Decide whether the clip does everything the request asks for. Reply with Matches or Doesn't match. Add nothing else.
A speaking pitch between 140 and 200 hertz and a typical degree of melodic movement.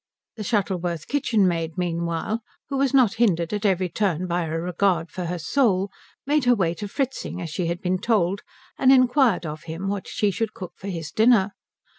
Matches